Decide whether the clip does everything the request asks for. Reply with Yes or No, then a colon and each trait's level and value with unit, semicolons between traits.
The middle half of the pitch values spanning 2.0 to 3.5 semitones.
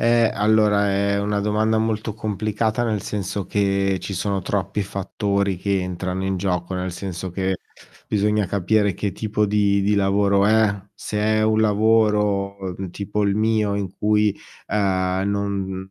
No: narrow, 1.6 semitones